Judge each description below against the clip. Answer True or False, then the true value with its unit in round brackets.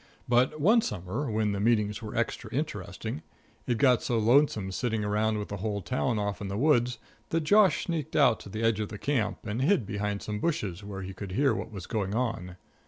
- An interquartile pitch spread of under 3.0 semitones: False (3.8 semitones)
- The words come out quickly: True (215 wpm)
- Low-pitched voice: True (110 Hz)